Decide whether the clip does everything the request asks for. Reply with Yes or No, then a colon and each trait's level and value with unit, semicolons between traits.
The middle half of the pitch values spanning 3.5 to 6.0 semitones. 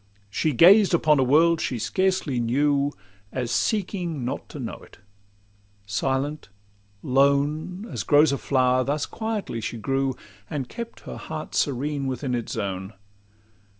Yes: average, 3.9 semitones